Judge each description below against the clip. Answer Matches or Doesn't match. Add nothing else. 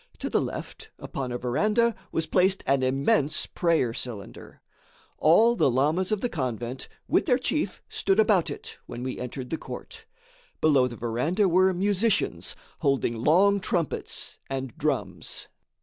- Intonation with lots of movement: Matches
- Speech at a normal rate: Matches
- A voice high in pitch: Doesn't match